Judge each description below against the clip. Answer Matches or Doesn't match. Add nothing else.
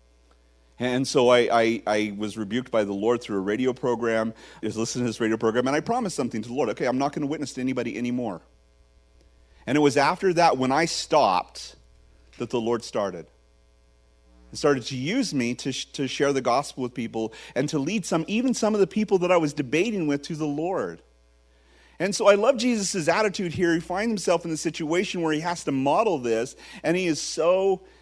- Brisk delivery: Matches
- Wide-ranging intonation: Matches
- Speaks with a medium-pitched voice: Doesn't match